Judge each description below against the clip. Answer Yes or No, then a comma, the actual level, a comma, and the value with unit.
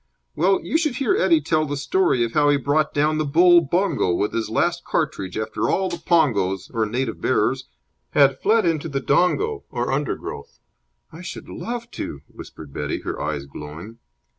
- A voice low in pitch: No, medium, 145 Hz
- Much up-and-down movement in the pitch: Yes, wide, 8.3 semitones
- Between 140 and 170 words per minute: No, average, 180 wpm